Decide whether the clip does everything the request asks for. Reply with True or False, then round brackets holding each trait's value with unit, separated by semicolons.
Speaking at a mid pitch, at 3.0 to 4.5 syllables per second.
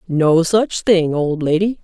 True (175 Hz; 3.6 syllables/s)